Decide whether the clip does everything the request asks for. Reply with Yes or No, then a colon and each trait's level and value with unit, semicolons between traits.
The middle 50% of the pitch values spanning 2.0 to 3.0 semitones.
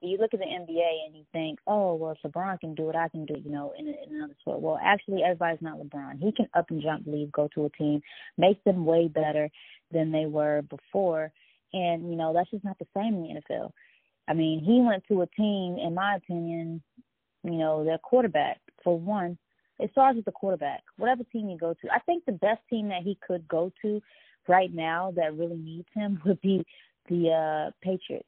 No: average, 4.0 semitones